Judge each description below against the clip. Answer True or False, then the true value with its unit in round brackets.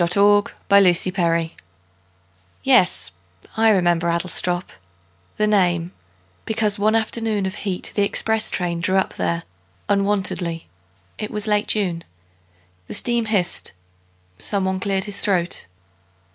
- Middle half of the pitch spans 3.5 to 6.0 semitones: False (3.1 semitones)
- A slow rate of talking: True (115 wpm)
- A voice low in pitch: False (195 Hz)